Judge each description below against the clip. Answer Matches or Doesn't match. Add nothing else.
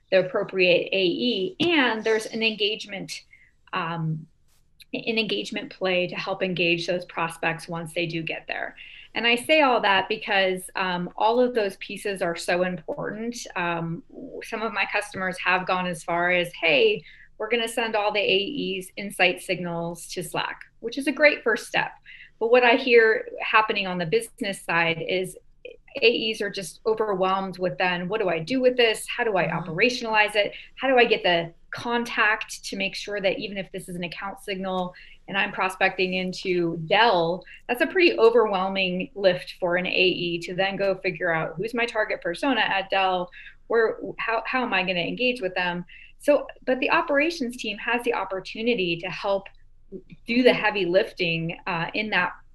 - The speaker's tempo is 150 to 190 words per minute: Matches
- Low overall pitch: Doesn't match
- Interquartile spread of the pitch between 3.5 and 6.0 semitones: Matches